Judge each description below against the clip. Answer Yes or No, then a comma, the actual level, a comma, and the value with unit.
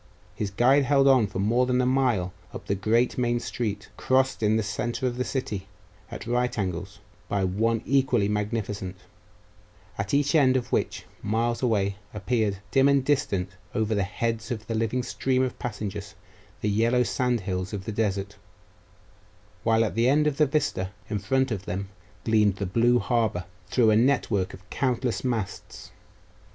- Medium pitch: No, low, 115 Hz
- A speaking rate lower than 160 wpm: No, average, 170 wpm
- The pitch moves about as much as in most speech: Yes, average, 3.8 semitones